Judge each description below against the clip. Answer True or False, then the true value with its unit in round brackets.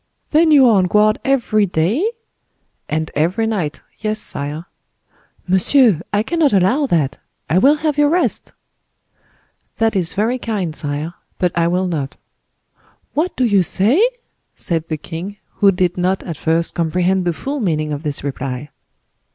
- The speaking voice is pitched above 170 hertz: True (185 Hz)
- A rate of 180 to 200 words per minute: False (150 wpm)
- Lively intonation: True (5.9 semitones)